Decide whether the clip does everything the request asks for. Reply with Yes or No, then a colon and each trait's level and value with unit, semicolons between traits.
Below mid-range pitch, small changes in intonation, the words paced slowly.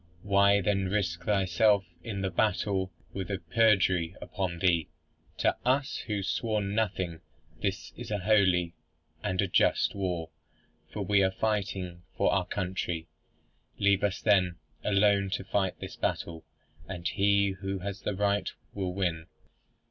No: very low, 95 Hz; narrow, 2.1 semitones; average, 150 wpm